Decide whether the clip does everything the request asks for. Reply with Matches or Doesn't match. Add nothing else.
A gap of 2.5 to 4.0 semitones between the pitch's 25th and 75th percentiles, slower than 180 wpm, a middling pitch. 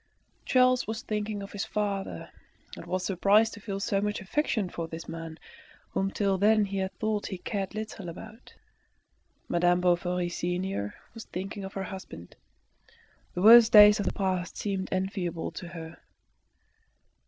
Doesn't match